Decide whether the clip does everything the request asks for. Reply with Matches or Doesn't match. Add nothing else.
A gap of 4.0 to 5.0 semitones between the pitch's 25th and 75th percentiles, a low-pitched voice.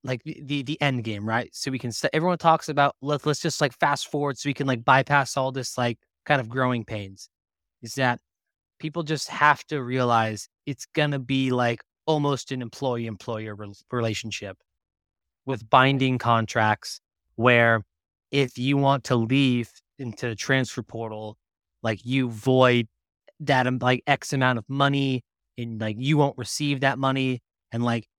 Doesn't match